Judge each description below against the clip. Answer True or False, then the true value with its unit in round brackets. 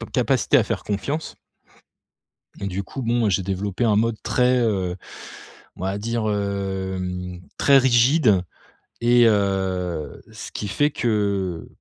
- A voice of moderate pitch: False (100 Hz)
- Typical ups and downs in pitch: True (3.8 semitones)